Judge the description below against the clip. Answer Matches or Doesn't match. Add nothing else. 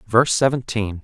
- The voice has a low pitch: Matches